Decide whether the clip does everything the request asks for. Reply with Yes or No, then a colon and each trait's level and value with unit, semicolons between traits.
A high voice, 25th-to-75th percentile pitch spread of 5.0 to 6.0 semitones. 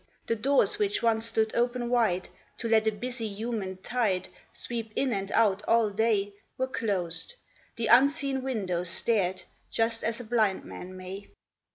No: high, 225 Hz; average, 3.4 semitones